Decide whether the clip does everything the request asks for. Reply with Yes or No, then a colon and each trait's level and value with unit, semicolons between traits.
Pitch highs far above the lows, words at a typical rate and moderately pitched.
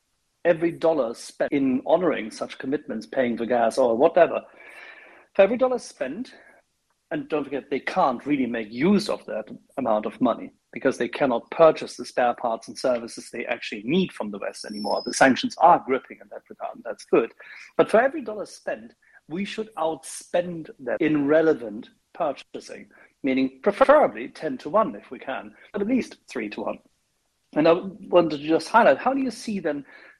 Yes: wide, 7.3 semitones; average, 185 wpm; medium, 165 Hz